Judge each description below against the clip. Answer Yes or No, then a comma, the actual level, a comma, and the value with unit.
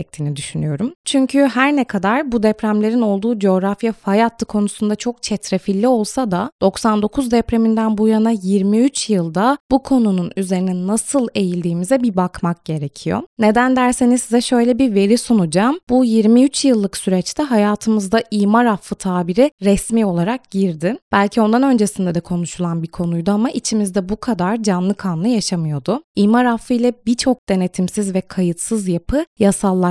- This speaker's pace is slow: No, fast, 140 wpm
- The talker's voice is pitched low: No, high, 215 Hz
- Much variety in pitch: No, average, 4.2 semitones